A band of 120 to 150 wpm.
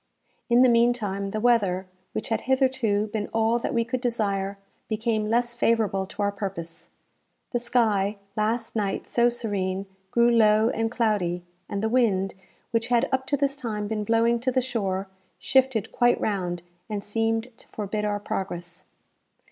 No: average, 165 wpm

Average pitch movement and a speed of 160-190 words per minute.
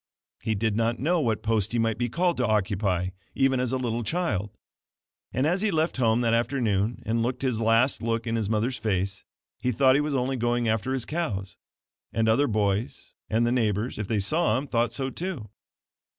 No: average, 3.3 semitones; fast, 205 wpm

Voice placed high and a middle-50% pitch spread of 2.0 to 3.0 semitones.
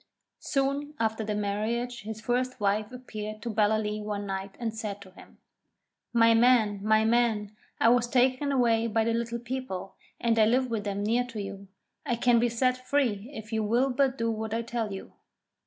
Yes: high, 225 Hz; narrow, 2.5 semitones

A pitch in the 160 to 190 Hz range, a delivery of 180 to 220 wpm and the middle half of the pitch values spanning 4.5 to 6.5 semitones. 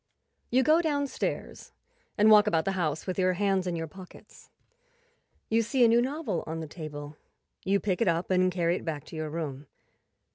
Yes: medium, 185 Hz; average, 190 wpm; average, 5.1 semitones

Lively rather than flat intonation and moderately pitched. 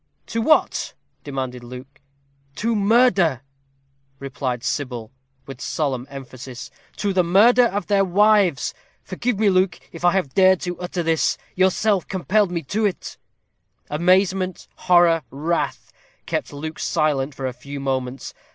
Yes: wide, 6.2 semitones; medium, 170 Hz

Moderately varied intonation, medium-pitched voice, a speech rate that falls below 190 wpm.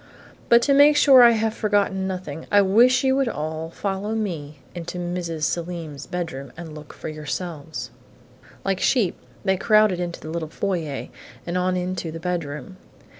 Yes: average, 4.2 semitones; medium, 180 Hz; average, 165 wpm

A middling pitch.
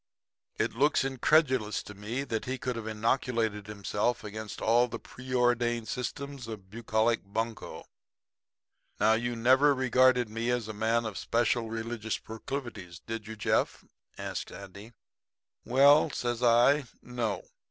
No: low, 115 Hz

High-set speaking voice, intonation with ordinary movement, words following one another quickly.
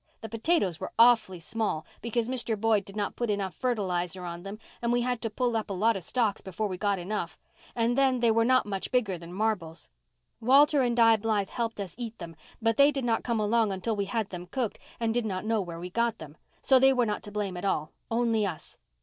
Yes: high, 220 Hz; average, 3.6 semitones; fast, 235 wpm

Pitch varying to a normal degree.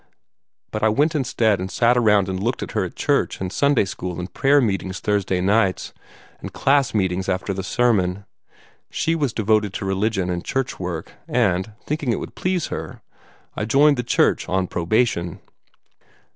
Yes: average, 4.8 semitones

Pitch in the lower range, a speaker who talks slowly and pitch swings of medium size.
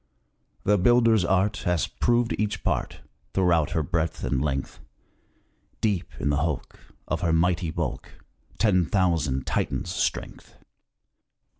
Yes: very low, 90 Hz; slow, 125 wpm; average, 4.2 semitones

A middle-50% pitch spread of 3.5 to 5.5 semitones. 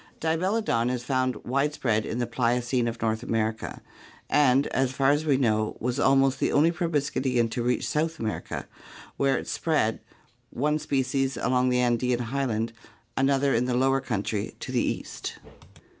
No: average, 2.8 semitones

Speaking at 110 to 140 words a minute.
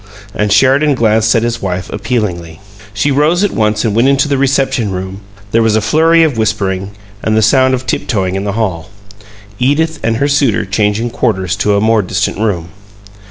No: average, 195 wpm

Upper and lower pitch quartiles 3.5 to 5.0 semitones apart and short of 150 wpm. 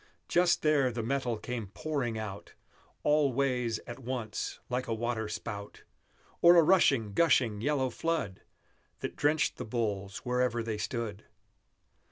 Yes: average, 4.0 semitones; average, 140 wpm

